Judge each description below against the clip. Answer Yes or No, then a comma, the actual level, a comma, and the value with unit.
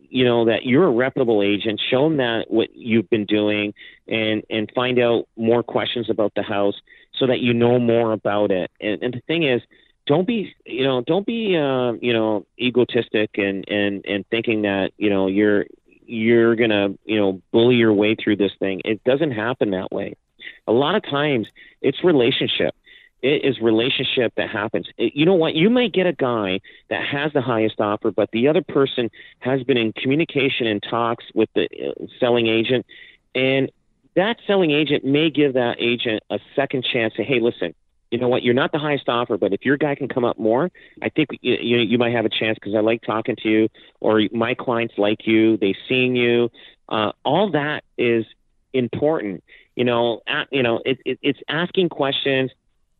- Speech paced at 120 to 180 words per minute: No, average, 200 wpm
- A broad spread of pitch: No, average, 3.2 semitones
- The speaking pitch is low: Yes, low, 120 Hz